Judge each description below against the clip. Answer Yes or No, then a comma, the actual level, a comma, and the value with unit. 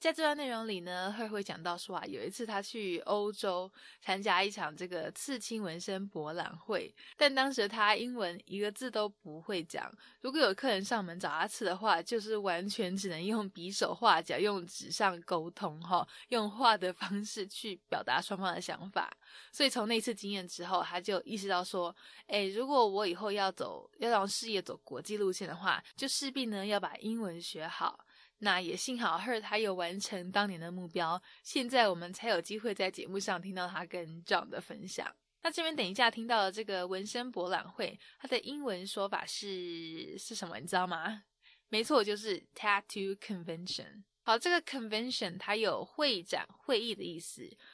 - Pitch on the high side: Yes, high, 200 Hz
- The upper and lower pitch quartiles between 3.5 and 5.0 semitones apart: Yes, average, 3.8 semitones